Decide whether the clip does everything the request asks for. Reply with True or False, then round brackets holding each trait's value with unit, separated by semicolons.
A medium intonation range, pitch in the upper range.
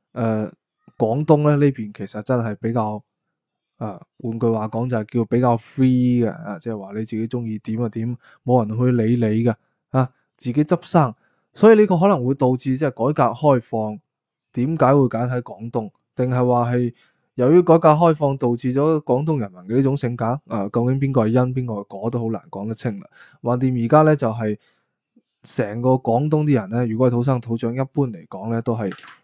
False (3.0 semitones; 120 Hz)